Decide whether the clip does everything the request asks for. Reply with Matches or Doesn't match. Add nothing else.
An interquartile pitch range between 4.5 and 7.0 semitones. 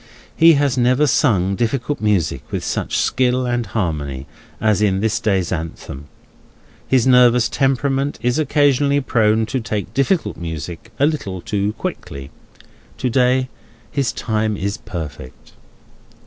Matches